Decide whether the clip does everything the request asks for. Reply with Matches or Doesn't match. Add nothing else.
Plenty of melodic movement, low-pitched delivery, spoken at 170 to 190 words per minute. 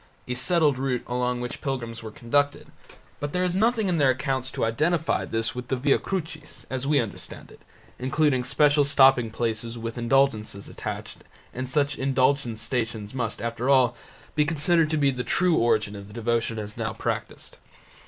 Doesn't match